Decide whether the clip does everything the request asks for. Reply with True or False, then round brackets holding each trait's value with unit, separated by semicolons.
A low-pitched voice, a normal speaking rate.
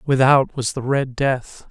True (130 Hz; 175 wpm)